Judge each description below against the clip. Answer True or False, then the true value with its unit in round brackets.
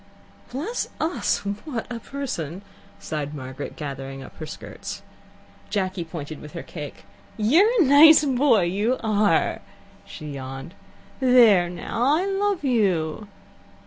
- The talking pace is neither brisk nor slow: False (125 wpm)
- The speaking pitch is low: False (205 Hz)